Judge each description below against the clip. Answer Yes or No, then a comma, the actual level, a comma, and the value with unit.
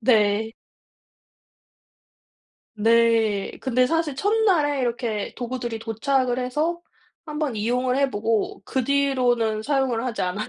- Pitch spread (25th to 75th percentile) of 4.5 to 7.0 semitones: No, average, 3.6 semitones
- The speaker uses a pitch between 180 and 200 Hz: No, high, 245 Hz